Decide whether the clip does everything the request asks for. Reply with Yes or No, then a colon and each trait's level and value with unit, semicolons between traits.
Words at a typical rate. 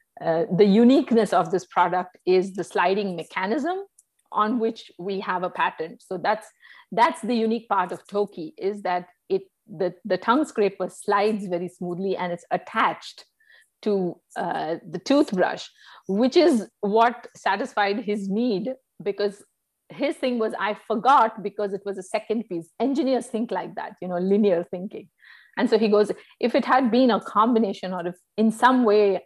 Yes: average, 170 wpm